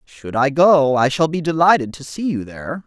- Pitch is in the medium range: Yes, medium, 145 Hz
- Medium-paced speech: No, fast, 230 wpm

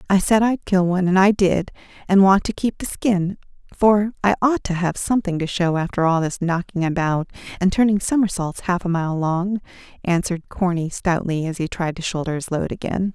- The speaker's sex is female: Yes, female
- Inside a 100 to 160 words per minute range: No, fast, 205 wpm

